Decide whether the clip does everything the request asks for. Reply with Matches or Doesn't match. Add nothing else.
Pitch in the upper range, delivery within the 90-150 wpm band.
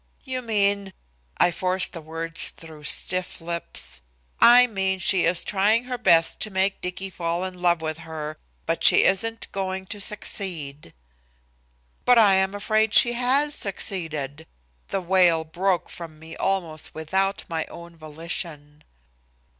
Doesn't match